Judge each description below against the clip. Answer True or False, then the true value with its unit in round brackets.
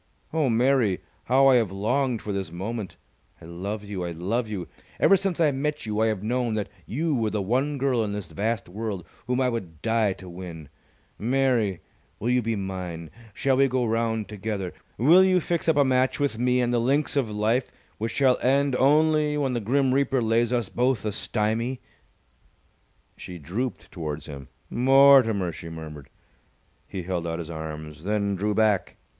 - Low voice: True (115 Hz)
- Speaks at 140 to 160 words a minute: False (185 wpm)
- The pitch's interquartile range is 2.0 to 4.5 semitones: False (5.3 semitones)